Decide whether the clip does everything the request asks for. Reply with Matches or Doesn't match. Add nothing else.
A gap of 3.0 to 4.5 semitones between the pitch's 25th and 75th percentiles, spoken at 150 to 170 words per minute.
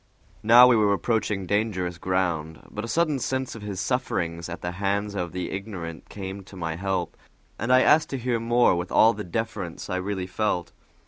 Doesn't match